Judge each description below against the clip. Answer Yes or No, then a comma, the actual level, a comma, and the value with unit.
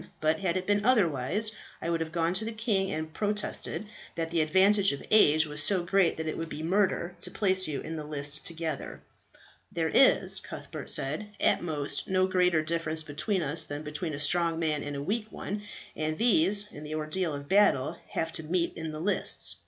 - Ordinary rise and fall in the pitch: Yes, average, 3.8 semitones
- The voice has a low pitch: No, medium, 165 Hz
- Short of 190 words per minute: No, fast, 205 wpm